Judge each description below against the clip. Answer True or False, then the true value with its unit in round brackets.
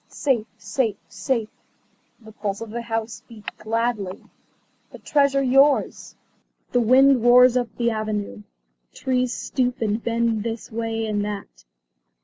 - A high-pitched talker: True (230 Hz)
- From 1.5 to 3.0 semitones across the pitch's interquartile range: True (2.5 semitones)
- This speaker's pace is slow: True (130 wpm)